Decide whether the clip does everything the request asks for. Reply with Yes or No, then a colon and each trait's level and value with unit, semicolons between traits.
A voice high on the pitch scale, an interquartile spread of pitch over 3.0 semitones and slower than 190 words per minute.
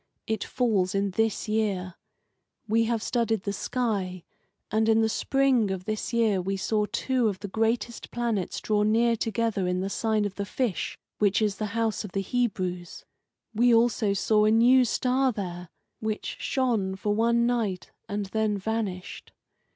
No: high, 215 Hz; average, 2.7 semitones; average, 165 wpm